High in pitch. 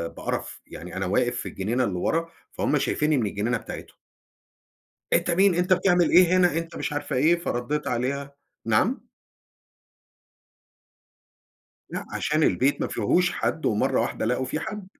No: medium, 145 Hz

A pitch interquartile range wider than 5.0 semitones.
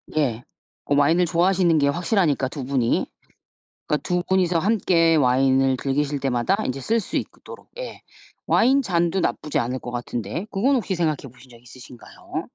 Yes: wide, 5.5 semitones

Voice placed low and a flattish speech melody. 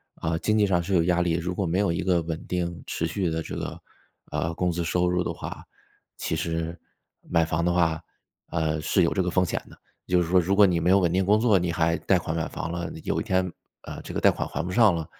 Yes: very low, 85 Hz; narrow, 1.8 semitones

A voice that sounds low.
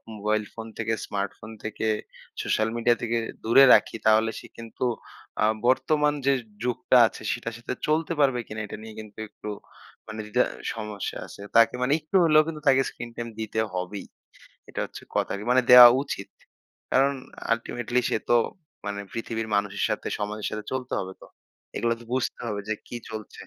Yes: low, 115 Hz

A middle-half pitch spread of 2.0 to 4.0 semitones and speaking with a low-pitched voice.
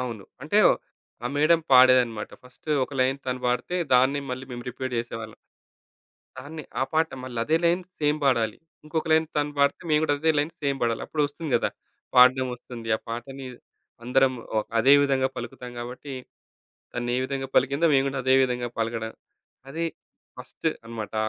Yes: average, 3.1 semitones; low, 130 Hz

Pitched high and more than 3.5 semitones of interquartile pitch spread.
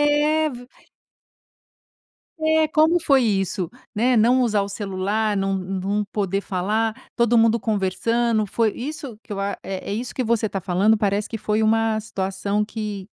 No: high, 215 Hz; average, 3.2 semitones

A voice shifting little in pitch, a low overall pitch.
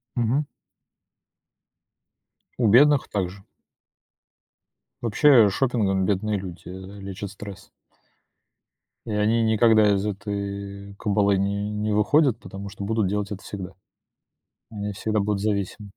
Yes: narrow, 1.7 semitones; low, 105 Hz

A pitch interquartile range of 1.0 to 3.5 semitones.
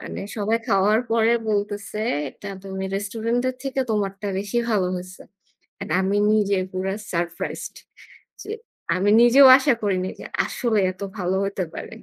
Yes: narrow, 2.6 semitones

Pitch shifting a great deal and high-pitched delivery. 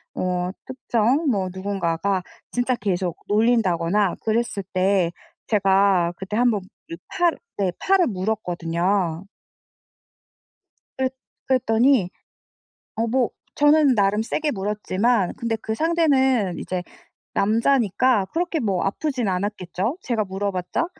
No: average, 4.8 semitones; high, 210 Hz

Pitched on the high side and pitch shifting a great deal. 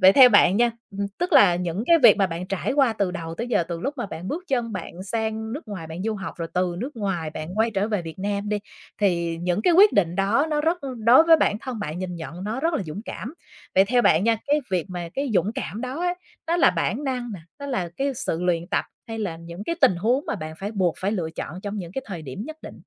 Yes: high, 205 Hz; wide, 5.9 semitones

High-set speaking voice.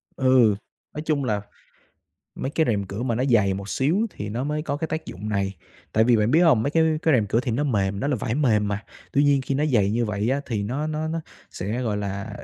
No: low, 120 Hz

